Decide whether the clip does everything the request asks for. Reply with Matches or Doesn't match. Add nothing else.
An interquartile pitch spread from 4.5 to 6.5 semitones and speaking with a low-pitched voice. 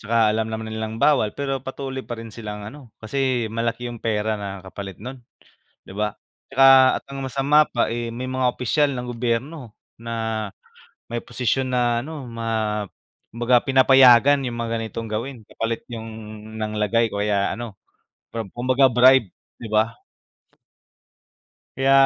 Doesn't match